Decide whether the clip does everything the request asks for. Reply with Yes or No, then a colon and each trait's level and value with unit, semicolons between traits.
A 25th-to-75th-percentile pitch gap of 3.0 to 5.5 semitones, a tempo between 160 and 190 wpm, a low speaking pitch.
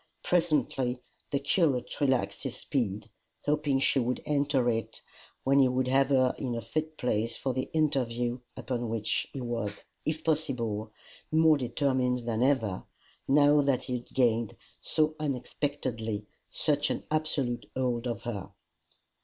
No: average, 3.4 semitones; average, 145 wpm; low, 130 Hz